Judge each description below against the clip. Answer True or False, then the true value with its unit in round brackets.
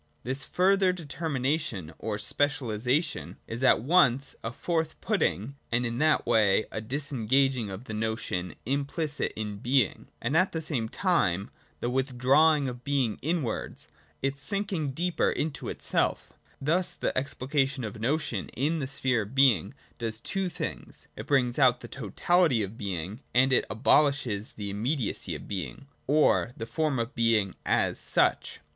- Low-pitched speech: True (130 Hz)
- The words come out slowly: False (155 wpm)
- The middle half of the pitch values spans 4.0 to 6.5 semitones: True (4.9 semitones)